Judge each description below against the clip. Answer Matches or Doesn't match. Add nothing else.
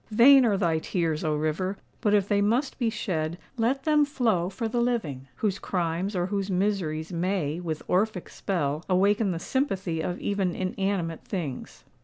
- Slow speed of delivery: Doesn't match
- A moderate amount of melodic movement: Matches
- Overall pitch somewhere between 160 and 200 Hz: Matches